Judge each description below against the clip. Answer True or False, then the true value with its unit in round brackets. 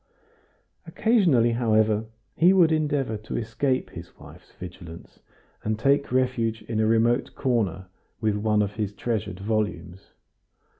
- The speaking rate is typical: False (130 wpm)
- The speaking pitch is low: True (110 Hz)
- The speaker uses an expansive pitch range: False (3.5 semitones)